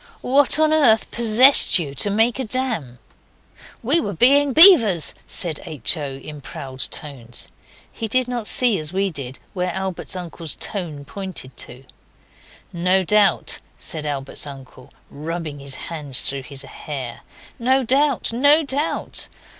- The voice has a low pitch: No, medium, 180 Hz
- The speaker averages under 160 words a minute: Yes, average, 145 wpm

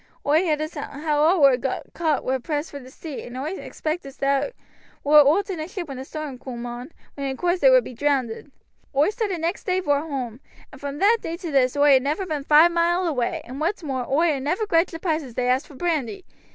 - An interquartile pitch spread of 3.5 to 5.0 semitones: Yes, average, 4.1 semitones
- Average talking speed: No, fast, 240 wpm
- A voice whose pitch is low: No, very high, 295 Hz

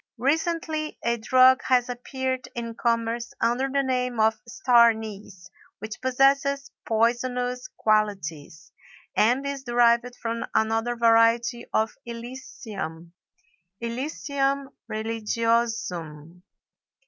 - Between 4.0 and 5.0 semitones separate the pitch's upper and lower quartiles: No, average, 2.8 semitones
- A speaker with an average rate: No, slow, 95 wpm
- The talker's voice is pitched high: Yes, high, 235 Hz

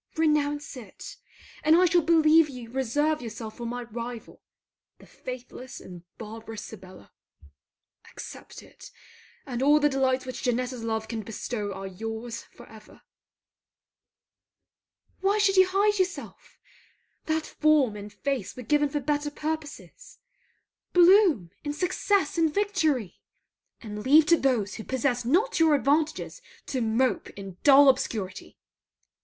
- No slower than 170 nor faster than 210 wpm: No, slow, 135 wpm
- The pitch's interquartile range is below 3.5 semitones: No, wide, 5.6 semitones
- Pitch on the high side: Yes, very high, 265 Hz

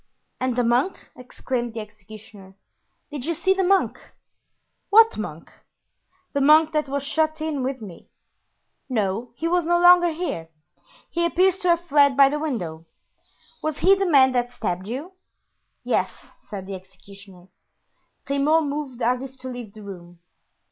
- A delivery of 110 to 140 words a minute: No, average, 155 wpm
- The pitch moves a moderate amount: No, wide, 6.7 semitones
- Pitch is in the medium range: No, very high, 265 Hz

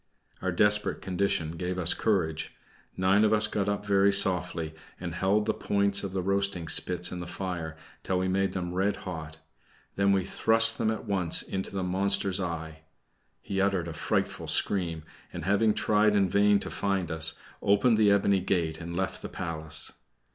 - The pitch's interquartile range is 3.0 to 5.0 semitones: No, narrow, 2.5 semitones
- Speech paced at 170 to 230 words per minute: Yes, average, 180 wpm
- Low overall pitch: Yes, very low, 95 Hz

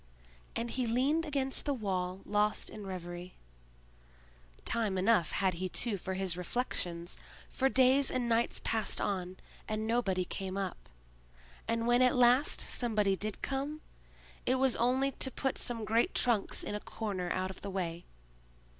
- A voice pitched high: Yes, high, 215 Hz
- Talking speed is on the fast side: No, average, 155 wpm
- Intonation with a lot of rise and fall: No, average, 4.9 semitones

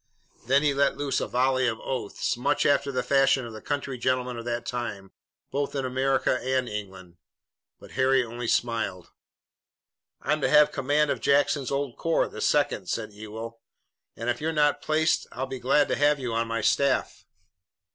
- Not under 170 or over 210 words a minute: Yes, average, 180 wpm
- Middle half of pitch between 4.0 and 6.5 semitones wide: No, average, 3.3 semitones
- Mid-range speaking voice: No, low, 130 Hz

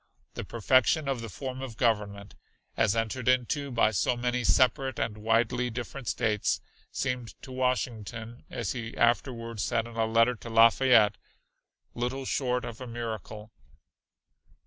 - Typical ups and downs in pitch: No, narrow, 2.2 semitones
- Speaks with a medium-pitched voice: No, low, 120 Hz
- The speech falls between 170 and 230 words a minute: No, average, 145 wpm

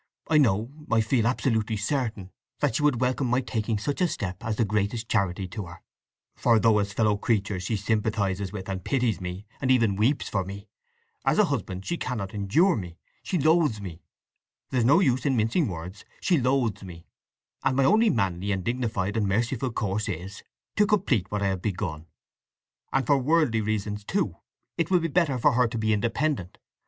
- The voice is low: Yes, low, 110 Hz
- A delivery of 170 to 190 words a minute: Yes, average, 185 wpm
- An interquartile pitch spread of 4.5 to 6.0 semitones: Yes, average, 4.8 semitones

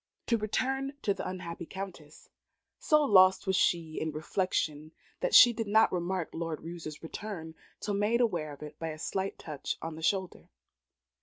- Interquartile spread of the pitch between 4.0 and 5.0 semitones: Yes, average, 4.4 semitones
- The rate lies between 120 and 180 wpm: Yes, average, 170 wpm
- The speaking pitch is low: No, medium, 180 Hz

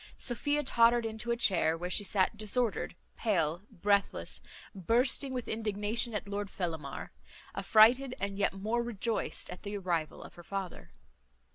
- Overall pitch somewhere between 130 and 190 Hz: No, high, 210 Hz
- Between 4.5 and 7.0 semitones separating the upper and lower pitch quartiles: No, average, 3.8 semitones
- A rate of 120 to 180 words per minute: Yes, average, 145 wpm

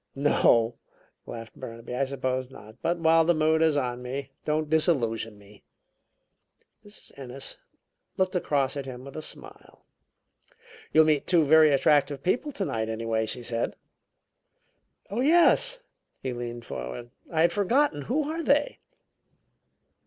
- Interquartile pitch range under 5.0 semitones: No, wide, 5.6 semitones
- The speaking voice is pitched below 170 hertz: Yes, medium, 140 Hz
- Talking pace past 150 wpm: No, average, 140 wpm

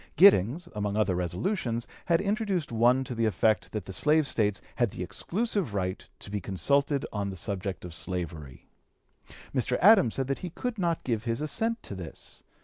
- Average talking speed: Yes, average, 180 wpm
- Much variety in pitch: Yes, wide, 8.4 semitones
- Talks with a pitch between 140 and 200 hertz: No, low, 115 Hz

